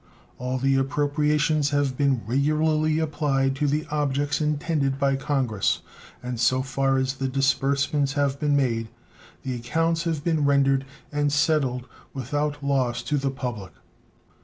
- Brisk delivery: No, average, 140 wpm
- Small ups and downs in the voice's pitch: Yes, narrow, 2.0 semitones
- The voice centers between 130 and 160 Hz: Yes, medium, 140 Hz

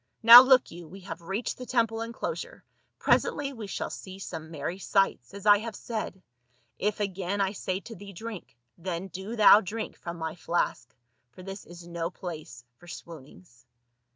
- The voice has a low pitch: No, high, 190 Hz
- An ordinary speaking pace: Yes, average, 180 wpm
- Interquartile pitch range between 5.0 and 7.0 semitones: No, average, 4.1 semitones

